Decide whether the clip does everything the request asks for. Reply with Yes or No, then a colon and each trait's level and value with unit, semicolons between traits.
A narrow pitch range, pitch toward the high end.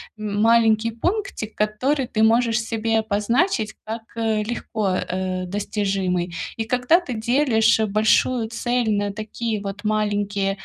Yes: narrow, 2.1 semitones; high, 220 Hz